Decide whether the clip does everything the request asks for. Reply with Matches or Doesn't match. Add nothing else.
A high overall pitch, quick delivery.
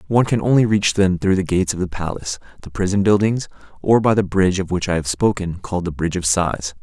Doesn't match